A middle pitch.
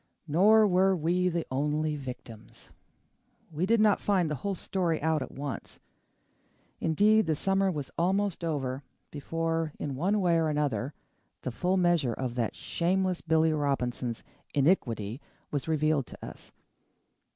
Yes: medium, 160 Hz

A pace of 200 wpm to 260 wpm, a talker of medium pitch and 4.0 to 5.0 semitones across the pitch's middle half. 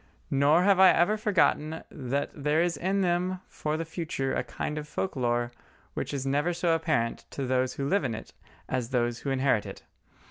Yes: fast, 205 wpm; medium, 150 Hz; average, 4.7 semitones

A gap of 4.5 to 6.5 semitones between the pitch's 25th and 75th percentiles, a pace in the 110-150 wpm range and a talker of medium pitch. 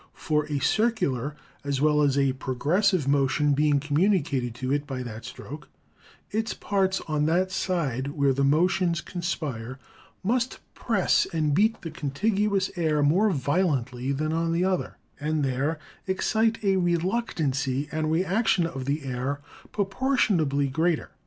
Yes: average, 5.2 semitones; average, 145 wpm; medium, 155 Hz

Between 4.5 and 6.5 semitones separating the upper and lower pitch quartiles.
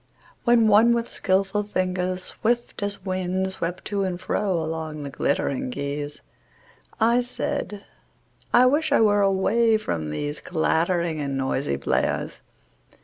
Yes: average, 5.0 semitones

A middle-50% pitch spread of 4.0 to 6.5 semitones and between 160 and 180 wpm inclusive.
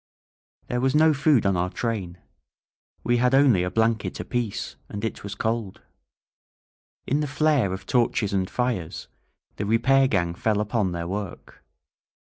No: average, 4.7 semitones; average, 150 wpm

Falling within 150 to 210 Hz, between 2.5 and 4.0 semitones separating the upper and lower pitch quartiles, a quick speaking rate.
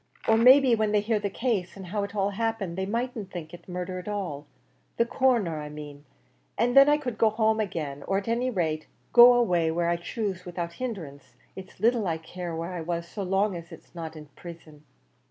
No: high, 190 Hz; average, 4.9 semitones; fast, 220 wpm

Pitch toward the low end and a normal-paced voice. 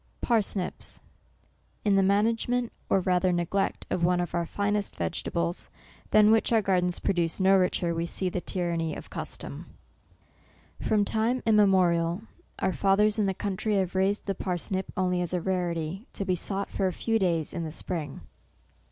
No: high, 190 Hz; average, 170 wpm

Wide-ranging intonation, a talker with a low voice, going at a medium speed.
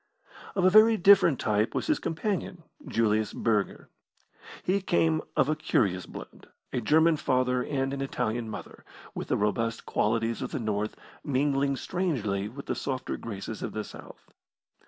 Yes: wide, 6.7 semitones; low, 130 Hz; average, 155 wpm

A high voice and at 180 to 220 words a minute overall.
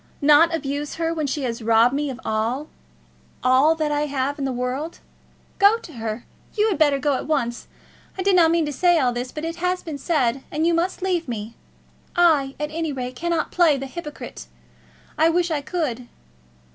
Yes: very high, 295 Hz; fast, 205 wpm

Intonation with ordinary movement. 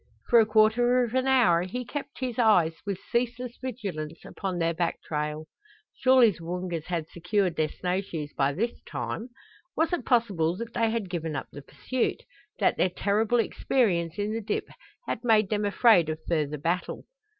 No: wide, 5.8 semitones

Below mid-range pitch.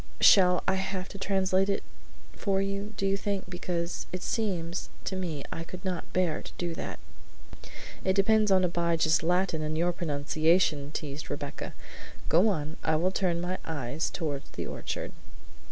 No: medium, 180 Hz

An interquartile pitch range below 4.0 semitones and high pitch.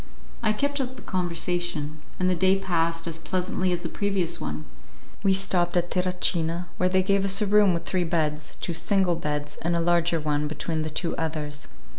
No: average, 2.7 semitones; medium, 175 Hz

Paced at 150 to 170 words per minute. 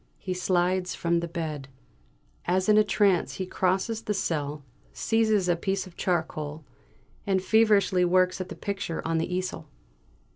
Yes: average, 155 wpm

